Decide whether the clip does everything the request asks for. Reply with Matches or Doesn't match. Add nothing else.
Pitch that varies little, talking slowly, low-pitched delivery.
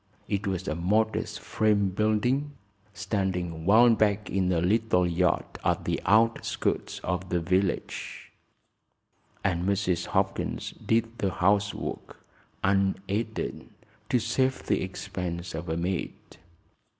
Doesn't match